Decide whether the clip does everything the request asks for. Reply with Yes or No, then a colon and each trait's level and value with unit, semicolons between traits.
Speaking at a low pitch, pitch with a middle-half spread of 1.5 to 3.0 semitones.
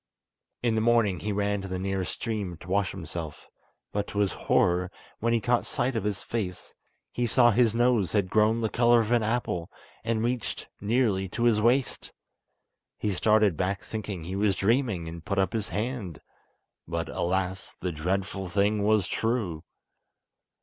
No: low, 105 Hz; average, 3.6 semitones